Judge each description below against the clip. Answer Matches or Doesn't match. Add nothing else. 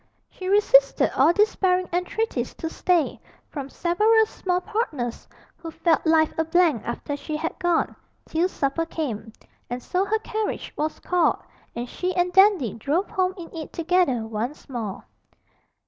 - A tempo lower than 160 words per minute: Matches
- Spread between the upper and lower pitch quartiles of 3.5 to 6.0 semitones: Matches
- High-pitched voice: Matches